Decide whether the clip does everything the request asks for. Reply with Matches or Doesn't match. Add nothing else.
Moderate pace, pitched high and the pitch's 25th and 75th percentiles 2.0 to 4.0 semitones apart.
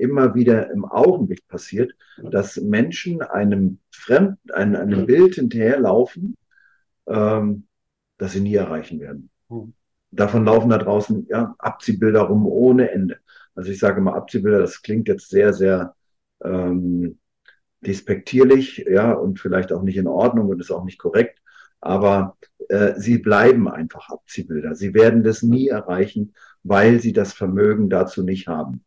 Doesn't match